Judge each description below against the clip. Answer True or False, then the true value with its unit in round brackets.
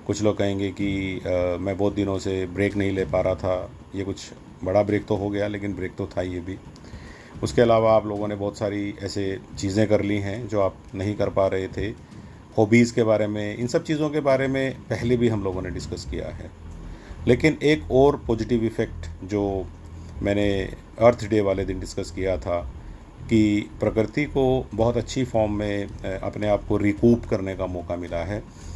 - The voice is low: True (100 Hz)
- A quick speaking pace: True (200 wpm)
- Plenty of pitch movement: False (2.9 semitones)